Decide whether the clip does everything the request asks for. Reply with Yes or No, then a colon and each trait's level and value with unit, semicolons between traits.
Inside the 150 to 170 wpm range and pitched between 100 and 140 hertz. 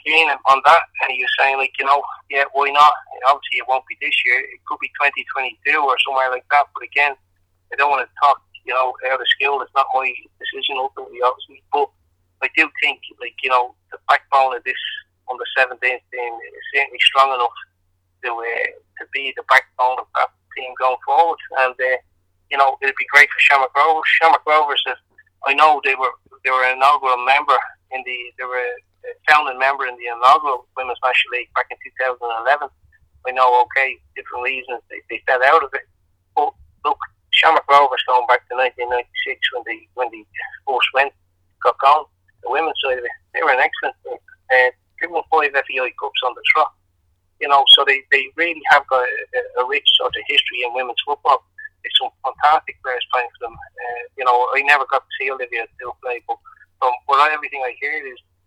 No: fast, 205 wpm; low, 135 Hz